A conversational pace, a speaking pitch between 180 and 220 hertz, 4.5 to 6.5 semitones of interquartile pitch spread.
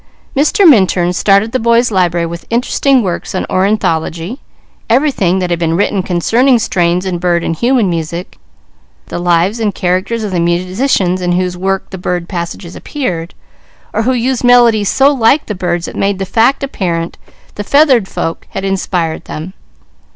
Yes: average, 165 wpm; high, 190 Hz; average, 5.0 semitones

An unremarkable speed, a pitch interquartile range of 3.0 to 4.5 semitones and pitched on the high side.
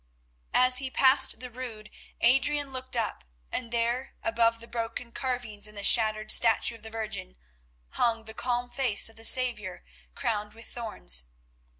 No: average, 160 wpm; narrow, 2.6 semitones; high, 230 Hz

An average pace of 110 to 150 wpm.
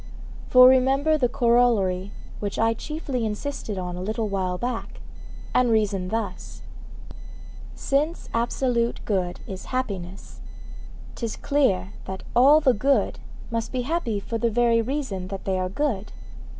Yes: slow, 135 wpm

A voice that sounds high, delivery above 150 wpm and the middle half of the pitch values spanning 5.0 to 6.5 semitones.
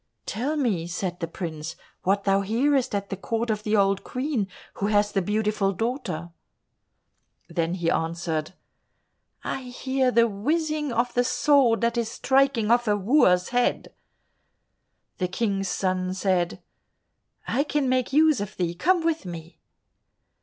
No: high, 210 Hz; average, 145 wpm; wide, 5.5 semitones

